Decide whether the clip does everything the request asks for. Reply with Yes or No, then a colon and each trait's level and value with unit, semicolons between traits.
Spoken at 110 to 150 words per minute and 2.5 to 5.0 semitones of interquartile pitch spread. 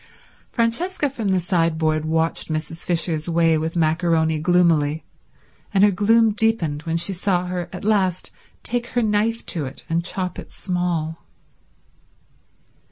Yes: average, 140 wpm; average, 4.1 semitones